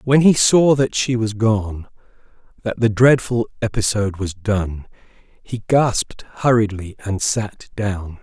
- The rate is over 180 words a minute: No, average, 140 wpm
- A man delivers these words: Yes, male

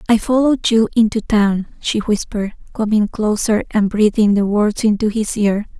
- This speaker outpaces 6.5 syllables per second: No, 4.9 syllables/s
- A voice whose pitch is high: Yes, high, 215 Hz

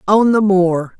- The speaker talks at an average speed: Yes, average, 180 wpm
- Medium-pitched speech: No, high, 195 Hz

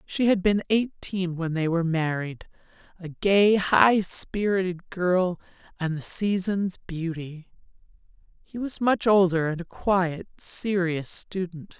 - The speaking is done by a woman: Yes, female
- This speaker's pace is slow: Yes, slow, 125 wpm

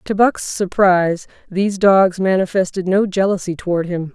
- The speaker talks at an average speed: Yes, average, 145 wpm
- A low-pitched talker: No, high, 190 Hz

